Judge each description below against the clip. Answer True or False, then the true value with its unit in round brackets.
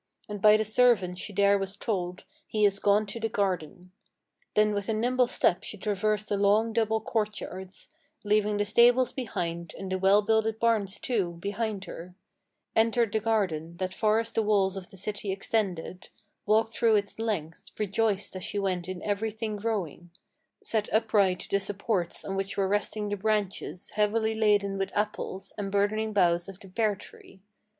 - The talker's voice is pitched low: False (205 Hz)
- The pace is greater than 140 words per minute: True (175 wpm)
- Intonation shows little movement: True (2.2 semitones)